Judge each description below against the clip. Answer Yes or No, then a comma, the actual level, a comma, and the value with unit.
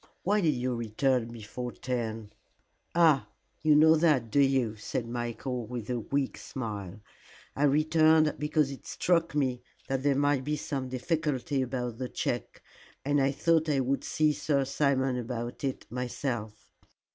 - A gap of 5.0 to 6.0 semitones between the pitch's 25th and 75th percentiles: No, average, 3.4 semitones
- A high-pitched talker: No, low, 135 Hz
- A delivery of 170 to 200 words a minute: No, average, 155 wpm